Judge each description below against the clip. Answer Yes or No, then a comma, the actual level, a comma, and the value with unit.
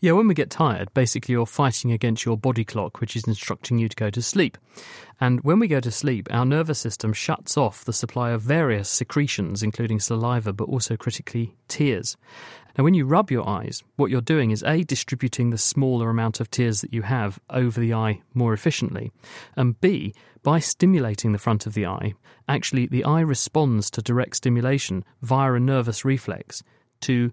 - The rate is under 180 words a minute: No, average, 195 wpm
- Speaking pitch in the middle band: No, low, 120 Hz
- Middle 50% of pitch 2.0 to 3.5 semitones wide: Yes, average, 3.2 semitones